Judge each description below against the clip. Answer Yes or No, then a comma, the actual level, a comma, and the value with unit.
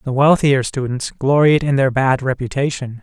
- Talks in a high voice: No, low, 135 Hz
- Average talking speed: Yes, average, 160 wpm